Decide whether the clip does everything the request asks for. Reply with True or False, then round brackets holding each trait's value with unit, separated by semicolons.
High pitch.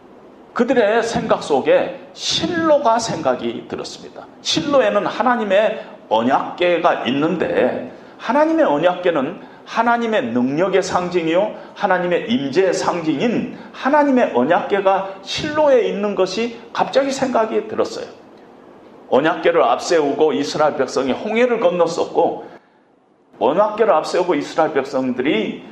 True (230 Hz)